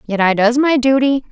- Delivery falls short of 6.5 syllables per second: Yes, 5.3 syllables/s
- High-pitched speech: Yes, high, 245 Hz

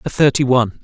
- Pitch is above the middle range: No, low, 130 Hz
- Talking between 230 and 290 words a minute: No, fast, 215 wpm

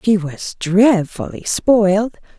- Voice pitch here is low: No, high, 200 Hz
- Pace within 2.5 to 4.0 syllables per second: Yes, 3.5 syllables/s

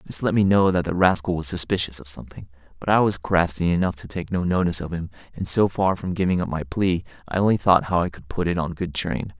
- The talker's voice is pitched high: No, very low, 85 Hz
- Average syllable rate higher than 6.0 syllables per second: Yes, 6.2 syllables/s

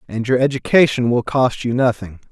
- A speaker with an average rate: Yes, average, 180 wpm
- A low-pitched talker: Yes, low, 120 Hz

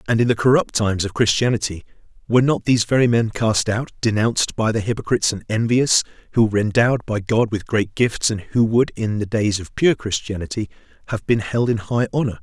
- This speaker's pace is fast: Yes, fast, 210 wpm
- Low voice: Yes, low, 110 Hz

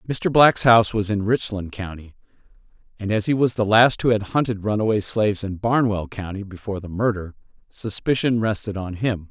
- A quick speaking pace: No, average, 180 wpm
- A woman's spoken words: No, male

